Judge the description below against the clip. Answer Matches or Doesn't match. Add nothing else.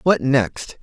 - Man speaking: Matches